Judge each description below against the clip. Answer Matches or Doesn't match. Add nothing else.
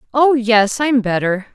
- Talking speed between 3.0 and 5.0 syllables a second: Matches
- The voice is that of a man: Doesn't match